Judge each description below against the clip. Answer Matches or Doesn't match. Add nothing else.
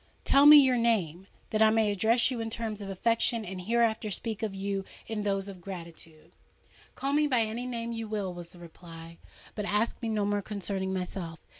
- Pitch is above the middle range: Matches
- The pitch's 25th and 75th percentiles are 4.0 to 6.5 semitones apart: Doesn't match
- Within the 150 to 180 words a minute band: Doesn't match